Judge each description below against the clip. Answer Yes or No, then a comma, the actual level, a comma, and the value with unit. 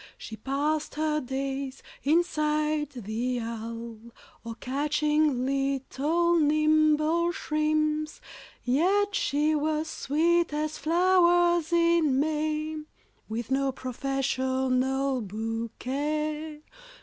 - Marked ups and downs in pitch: No, average, 2.9 semitones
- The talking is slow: Yes, slow, 85 wpm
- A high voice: Yes, very high, 300 Hz